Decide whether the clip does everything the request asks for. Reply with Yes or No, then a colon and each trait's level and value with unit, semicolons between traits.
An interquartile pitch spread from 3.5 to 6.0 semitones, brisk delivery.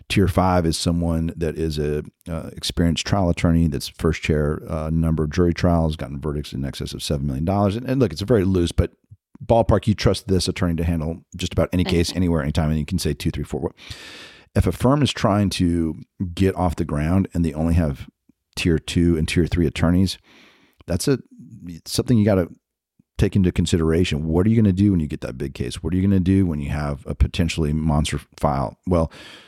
No: average, 2.9 semitones; fast, 225 wpm